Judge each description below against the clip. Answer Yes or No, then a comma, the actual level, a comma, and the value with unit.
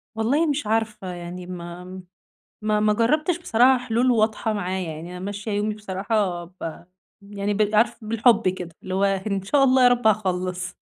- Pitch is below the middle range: No, high, 210 Hz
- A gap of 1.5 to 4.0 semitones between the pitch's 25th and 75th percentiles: Yes, average, 3.6 semitones